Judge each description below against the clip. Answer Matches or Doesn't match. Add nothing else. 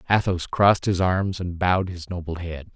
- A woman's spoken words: Doesn't match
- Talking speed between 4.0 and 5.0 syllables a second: Doesn't match